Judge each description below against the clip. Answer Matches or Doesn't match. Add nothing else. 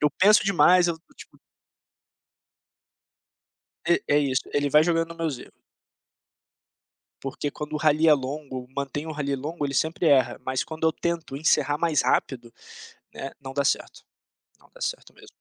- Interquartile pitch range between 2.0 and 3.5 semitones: Matches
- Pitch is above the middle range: Doesn't match